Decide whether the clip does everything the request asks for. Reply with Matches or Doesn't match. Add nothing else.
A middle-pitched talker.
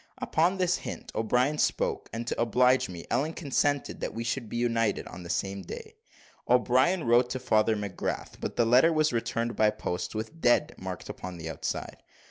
Doesn't match